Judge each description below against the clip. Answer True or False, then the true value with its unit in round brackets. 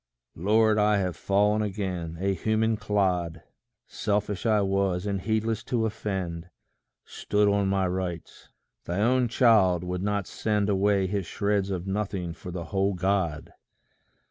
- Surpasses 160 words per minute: False (145 wpm)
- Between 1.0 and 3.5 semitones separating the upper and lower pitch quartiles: True (2.4 semitones)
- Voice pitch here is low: True (100 Hz)